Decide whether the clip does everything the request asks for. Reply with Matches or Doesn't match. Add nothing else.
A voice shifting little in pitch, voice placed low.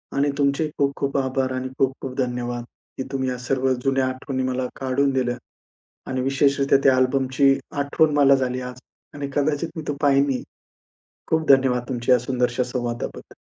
Matches